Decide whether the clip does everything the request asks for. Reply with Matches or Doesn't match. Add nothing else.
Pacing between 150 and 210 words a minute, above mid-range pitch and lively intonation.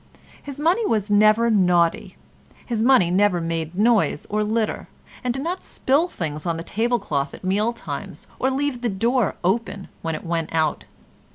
Matches